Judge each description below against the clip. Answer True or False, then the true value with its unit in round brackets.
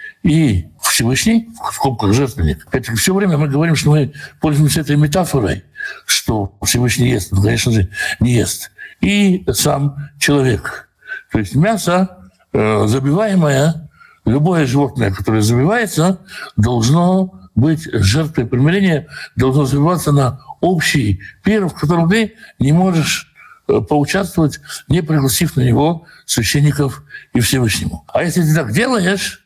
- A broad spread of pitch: True (6.0 semitones)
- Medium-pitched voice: True (145 Hz)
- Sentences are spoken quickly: False (125 wpm)